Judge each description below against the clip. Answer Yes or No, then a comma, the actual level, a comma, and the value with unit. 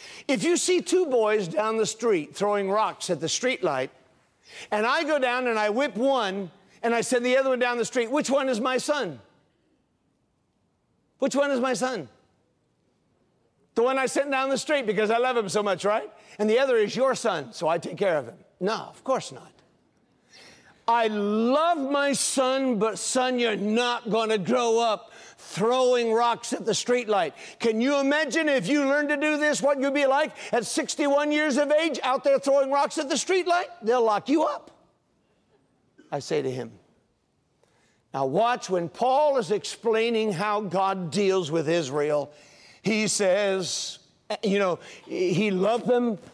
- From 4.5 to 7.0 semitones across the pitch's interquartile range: Yes, average, 4.9 semitones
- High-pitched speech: Yes, high, 240 Hz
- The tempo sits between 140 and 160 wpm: No, average, 180 wpm